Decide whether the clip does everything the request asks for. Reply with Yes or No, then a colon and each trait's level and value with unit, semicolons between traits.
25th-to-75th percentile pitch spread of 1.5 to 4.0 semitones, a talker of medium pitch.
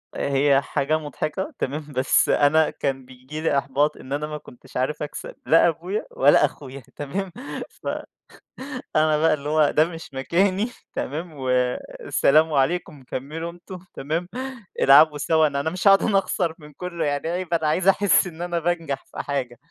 Yes: average, 3.3 semitones; medium, 155 Hz